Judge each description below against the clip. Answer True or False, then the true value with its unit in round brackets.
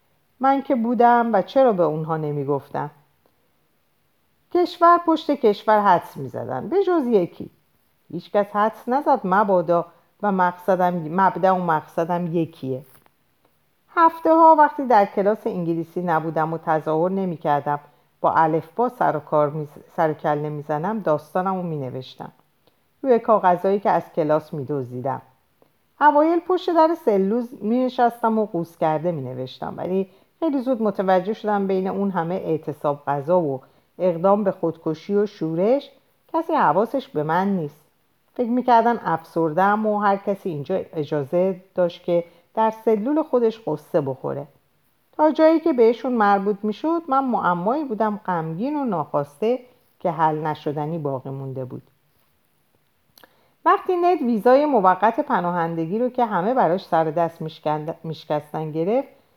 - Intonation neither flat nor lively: False (6.9 semitones)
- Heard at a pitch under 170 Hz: False (185 Hz)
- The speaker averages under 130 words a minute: False (140 wpm)